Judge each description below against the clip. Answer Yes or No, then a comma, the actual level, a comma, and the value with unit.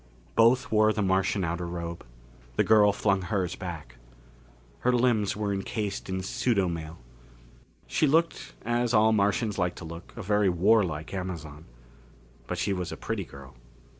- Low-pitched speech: Yes, very low, 95 Hz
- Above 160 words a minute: No, average, 150 wpm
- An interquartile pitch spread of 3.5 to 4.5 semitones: Yes, average, 4.0 semitones